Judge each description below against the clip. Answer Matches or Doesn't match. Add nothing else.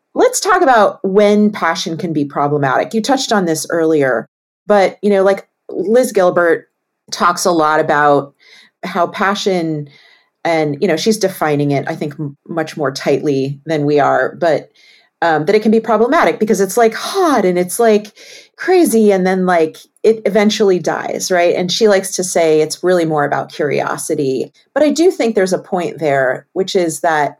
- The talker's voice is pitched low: Doesn't match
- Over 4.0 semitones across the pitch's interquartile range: Matches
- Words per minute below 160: Doesn't match